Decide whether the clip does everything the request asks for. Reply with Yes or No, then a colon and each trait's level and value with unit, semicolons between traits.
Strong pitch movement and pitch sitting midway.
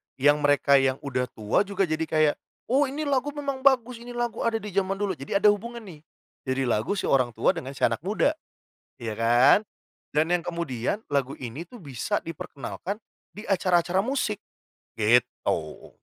Yes: wide, 8.0 semitones; medium, 170 Hz